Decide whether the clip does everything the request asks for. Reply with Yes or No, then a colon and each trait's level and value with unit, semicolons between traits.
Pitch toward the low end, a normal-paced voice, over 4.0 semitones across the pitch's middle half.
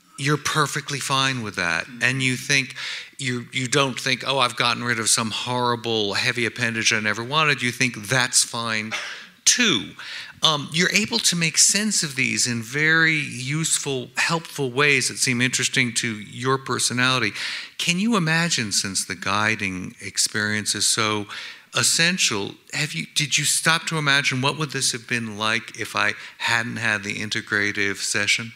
Yes: low, 125 Hz; average, 165 wpm; average, 4.7 semitones